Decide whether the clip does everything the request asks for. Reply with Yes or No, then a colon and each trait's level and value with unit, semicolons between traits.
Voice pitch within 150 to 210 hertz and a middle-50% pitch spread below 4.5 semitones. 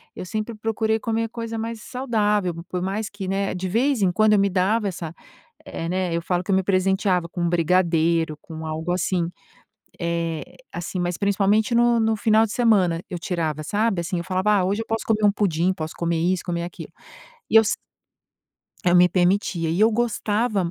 Yes: high, 190 Hz; average, 3.8 semitones